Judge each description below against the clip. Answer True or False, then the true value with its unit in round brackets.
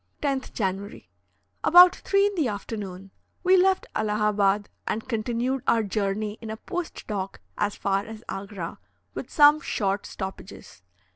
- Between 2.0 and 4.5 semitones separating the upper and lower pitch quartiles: False (5.3 semitones)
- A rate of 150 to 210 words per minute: False (140 wpm)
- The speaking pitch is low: False (215 Hz)